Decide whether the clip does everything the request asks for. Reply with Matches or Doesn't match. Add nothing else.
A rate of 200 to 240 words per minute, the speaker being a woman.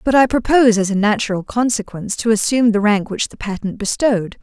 Matches